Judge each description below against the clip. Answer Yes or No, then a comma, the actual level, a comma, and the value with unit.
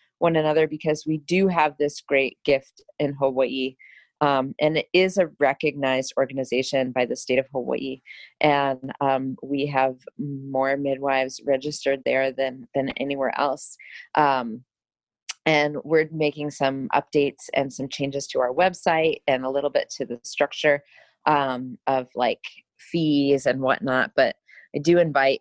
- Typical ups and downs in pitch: No, narrow, 2.2 semitones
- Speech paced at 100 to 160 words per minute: Yes, average, 150 wpm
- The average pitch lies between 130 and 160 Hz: Yes, medium, 140 Hz